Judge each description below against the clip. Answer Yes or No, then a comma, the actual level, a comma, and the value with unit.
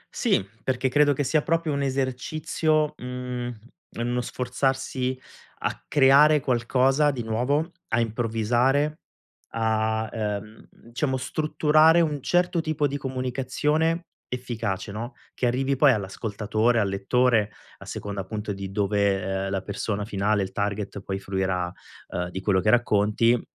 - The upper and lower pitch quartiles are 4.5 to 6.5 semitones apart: Yes, average, 4.8 semitones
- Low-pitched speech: Yes, low, 120 Hz